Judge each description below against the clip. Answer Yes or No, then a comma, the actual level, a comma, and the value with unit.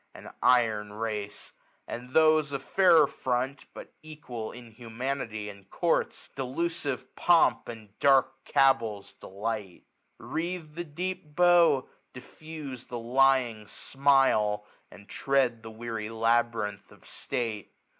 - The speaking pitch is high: No, low, 125 Hz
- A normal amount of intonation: Yes, average, 4.2 semitones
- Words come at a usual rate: No, slow, 115 wpm